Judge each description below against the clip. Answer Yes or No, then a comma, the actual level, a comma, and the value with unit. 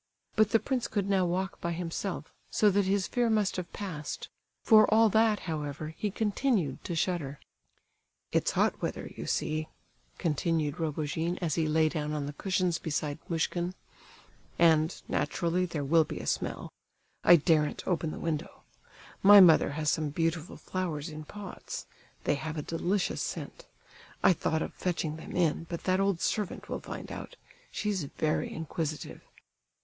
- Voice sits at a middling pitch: Yes, medium, 170 Hz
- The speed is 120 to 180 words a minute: Yes, average, 160 wpm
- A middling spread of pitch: Yes, average, 3.7 semitones